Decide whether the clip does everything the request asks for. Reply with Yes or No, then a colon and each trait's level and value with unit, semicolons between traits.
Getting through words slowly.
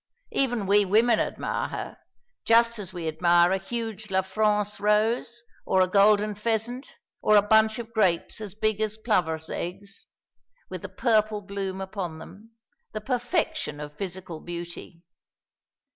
No: average, 145 wpm